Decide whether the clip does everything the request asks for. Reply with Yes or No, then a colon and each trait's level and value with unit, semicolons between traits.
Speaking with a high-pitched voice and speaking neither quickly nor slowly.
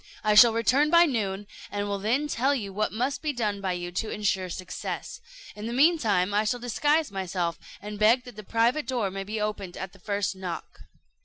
No: high, 210 Hz; fast, 215 wpm